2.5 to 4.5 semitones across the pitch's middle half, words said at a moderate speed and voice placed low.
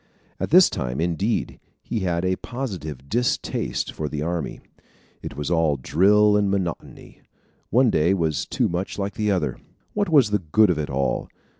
No: average, 5.3 semitones; average, 165 wpm; very low, 90 Hz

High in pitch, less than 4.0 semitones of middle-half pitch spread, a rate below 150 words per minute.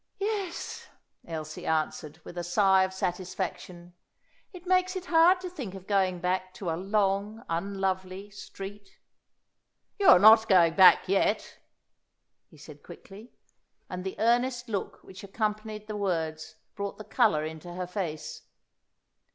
Yes: high, 195 Hz; average, 3.4 semitones; average, 140 wpm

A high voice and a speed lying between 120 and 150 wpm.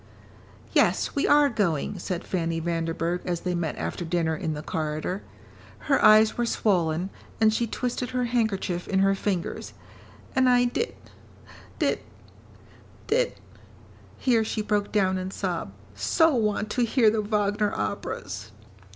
Yes: high, 200 Hz; average, 145 wpm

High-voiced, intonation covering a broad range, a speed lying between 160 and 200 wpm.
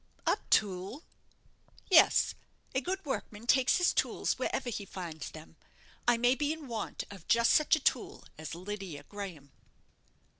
No: high, 215 Hz; wide, 6.4 semitones; average, 150 wpm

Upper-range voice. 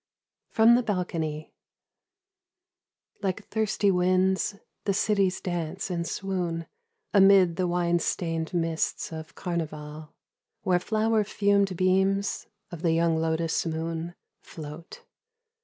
No: medium, 180 Hz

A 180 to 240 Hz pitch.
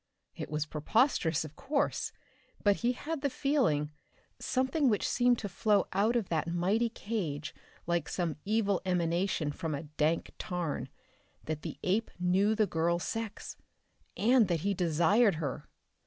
Yes: high, 190 Hz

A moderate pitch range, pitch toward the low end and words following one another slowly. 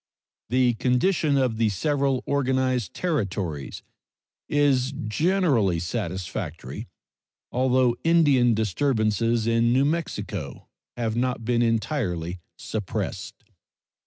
Yes: average, 4.4 semitones; low, 120 Hz; slow, 90 wpm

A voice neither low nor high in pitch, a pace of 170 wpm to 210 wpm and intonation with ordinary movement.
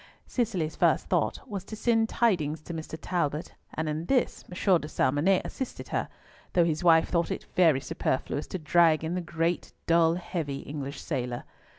Yes: medium, 165 Hz; average, 175 wpm; average, 3.1 semitones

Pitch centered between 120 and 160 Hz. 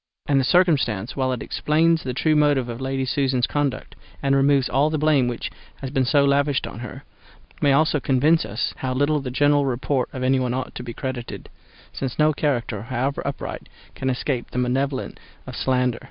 Yes: low, 135 Hz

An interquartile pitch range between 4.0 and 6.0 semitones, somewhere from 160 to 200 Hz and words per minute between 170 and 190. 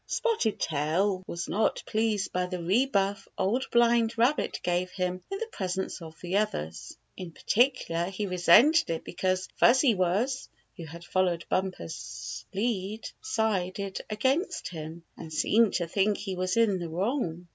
No: average, 4.4 semitones; high, 190 Hz; average, 155 wpm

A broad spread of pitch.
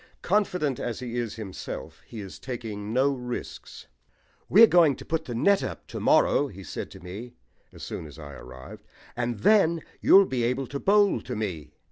Yes: wide, 6.8 semitones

